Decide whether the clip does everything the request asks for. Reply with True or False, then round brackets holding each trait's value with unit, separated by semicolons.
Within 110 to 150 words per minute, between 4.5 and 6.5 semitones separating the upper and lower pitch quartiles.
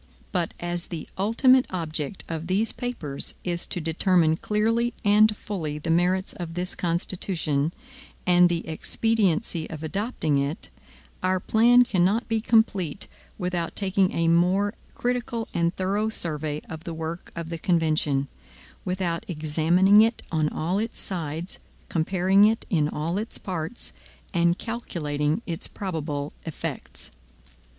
False (135 wpm; 4.1 semitones)